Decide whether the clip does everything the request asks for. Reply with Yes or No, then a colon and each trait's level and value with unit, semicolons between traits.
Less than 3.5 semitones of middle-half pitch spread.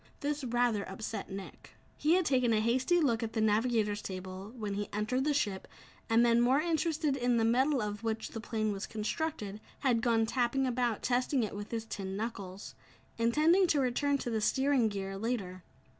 No: average, 3.9 semitones